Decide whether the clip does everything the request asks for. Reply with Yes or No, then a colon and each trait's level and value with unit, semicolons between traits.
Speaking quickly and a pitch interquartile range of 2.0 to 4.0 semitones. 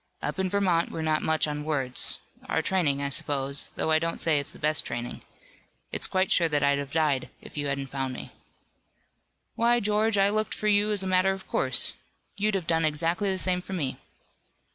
No: fast, 210 wpm; average, 5.0 semitones